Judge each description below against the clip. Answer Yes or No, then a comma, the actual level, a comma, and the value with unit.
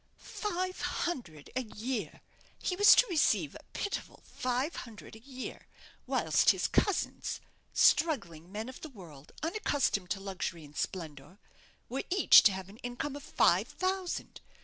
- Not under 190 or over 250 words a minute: No, average, 150 wpm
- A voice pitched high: Yes, high, 245 Hz